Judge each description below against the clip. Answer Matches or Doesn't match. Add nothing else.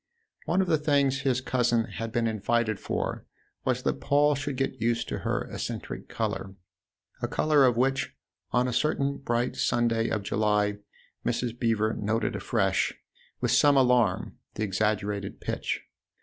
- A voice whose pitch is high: Doesn't match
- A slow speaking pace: Doesn't match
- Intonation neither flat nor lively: Matches